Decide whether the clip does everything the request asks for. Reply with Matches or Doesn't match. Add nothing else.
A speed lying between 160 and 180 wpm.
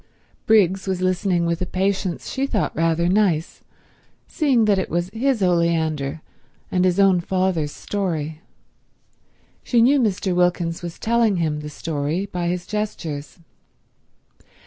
Doesn't match